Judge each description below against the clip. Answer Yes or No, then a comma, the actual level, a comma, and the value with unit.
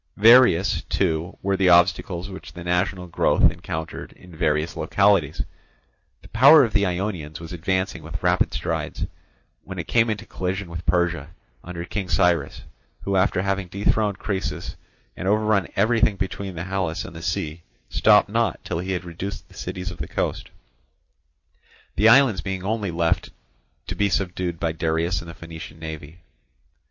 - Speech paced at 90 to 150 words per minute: No, average, 160 wpm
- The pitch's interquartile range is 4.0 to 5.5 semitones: No, average, 3.1 semitones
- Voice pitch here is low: Yes, very low, 90 Hz